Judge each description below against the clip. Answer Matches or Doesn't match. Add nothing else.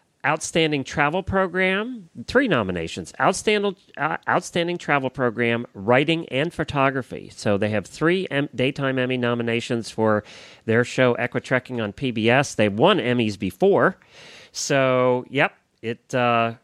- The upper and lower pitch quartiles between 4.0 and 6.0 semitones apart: Matches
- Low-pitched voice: Matches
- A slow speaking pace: Matches